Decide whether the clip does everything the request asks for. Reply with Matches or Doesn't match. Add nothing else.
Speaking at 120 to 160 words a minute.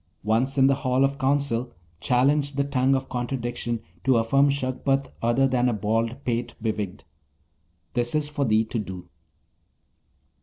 Matches